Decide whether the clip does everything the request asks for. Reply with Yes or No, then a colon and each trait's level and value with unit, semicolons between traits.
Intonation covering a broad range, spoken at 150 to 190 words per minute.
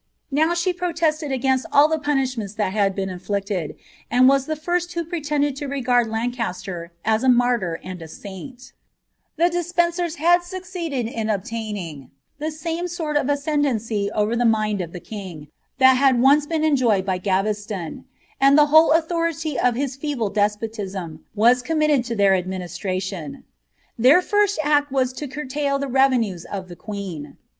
Yes: wide, 6.8 semitones; average, 165 wpm